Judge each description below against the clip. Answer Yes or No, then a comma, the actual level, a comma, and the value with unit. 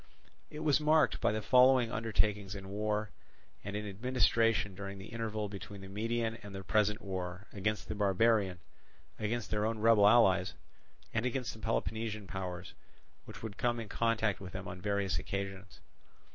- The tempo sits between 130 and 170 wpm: Yes, average, 165 wpm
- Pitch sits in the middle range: No, low, 105 Hz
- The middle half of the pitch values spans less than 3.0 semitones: Yes, narrow, 2.6 semitones